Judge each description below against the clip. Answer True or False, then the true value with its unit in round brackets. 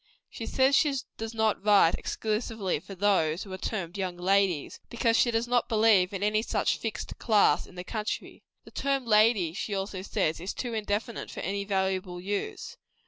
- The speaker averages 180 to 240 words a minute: True (185 wpm)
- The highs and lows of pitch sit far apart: False (3.0 semitones)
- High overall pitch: True (205 Hz)